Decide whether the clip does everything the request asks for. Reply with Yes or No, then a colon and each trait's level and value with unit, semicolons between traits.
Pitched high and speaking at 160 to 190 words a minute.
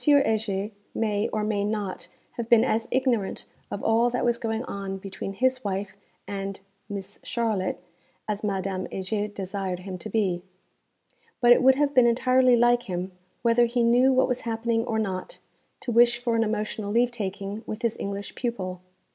Yes: high, 220 Hz; average, 170 wpm